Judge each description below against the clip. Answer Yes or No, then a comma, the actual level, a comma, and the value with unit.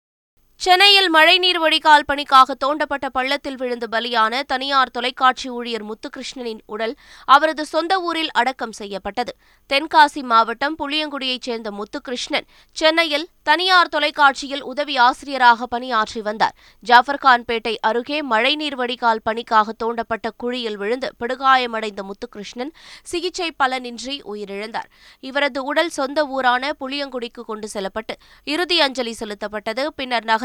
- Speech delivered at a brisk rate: No, average, 105 wpm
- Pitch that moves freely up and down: No, average, 4.1 semitones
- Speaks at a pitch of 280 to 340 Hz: No, very high, 260 Hz